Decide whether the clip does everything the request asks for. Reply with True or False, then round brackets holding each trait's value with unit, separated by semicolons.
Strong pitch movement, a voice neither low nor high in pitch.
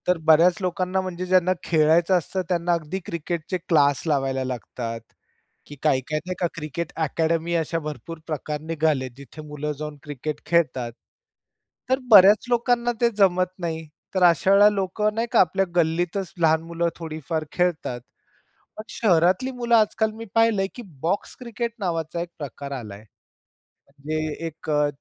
False (3.6 semitones; 170 Hz)